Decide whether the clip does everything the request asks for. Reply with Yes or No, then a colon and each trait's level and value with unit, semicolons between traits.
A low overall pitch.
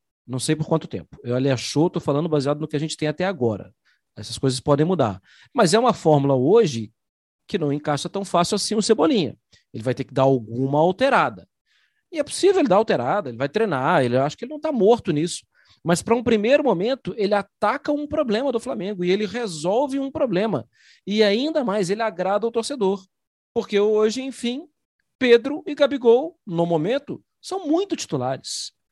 No: high, 195 Hz